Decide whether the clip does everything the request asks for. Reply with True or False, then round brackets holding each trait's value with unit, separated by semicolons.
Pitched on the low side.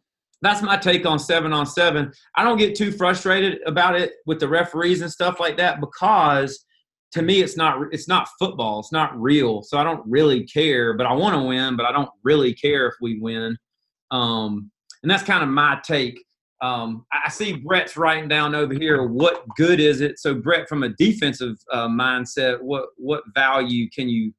False (150 Hz)